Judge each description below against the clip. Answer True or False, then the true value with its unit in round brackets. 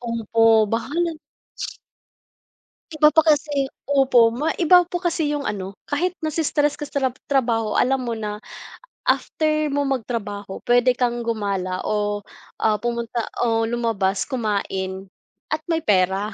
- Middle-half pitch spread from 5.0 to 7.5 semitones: True (5.5 semitones)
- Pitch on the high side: True (235 Hz)